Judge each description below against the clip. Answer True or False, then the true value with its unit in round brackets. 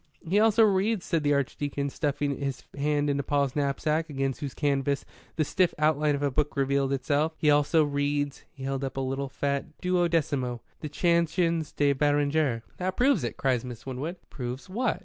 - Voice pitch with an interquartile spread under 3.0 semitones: True (2.6 semitones)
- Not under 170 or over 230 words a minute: True (180 wpm)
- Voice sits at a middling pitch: True (145 Hz)